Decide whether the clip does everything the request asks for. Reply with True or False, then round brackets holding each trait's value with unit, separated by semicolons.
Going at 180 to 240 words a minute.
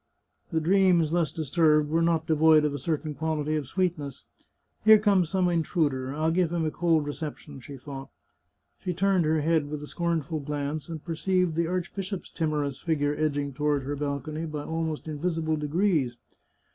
True (185 wpm)